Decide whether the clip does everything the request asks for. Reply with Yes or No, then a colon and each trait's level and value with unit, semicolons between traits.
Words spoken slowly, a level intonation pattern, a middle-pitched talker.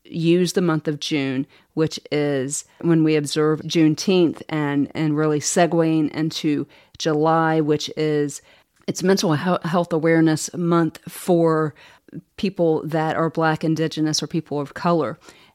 Yes: slow, 130 wpm; narrow, 1.6 semitones; medium, 160 Hz